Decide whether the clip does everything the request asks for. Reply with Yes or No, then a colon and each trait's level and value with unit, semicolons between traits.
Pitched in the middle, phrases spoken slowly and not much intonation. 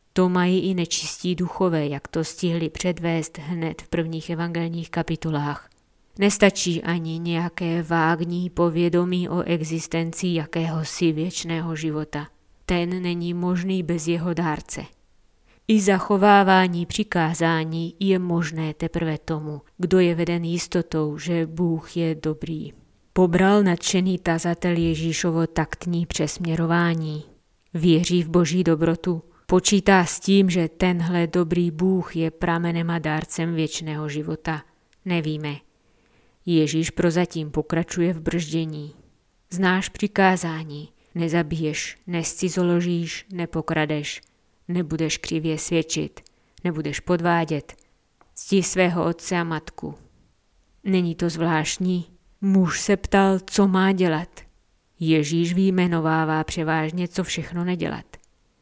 Yes: medium, 170 Hz; slow, 105 wpm; narrow, 1.9 semitones